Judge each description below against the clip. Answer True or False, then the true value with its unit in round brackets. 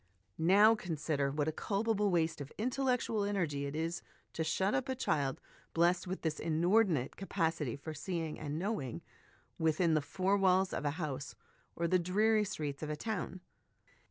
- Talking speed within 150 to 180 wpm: True (165 wpm)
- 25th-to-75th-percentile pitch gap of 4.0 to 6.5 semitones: True (4.7 semitones)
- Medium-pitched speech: True (170 Hz)